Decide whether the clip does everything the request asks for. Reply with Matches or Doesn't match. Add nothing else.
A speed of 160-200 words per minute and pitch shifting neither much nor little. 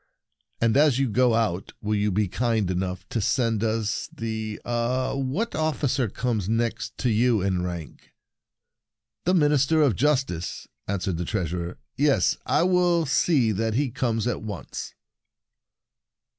Doesn't match